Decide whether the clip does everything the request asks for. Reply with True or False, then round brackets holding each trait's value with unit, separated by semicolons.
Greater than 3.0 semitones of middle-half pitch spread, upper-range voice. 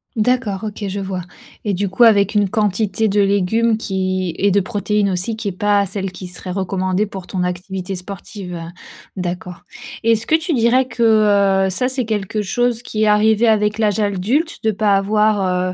False (2.5 semitones; 205 Hz)